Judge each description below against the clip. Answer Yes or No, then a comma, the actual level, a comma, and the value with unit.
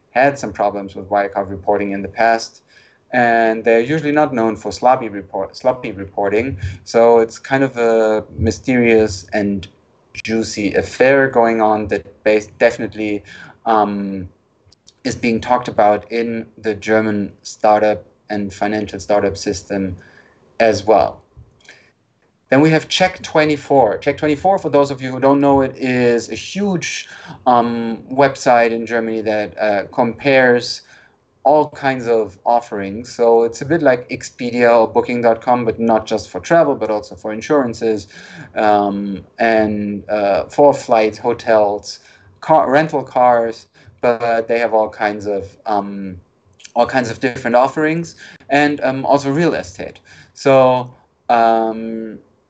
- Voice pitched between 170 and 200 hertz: No, low, 115 Hz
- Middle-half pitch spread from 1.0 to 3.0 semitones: No, average, 3.5 semitones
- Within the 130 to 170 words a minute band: Yes, average, 140 wpm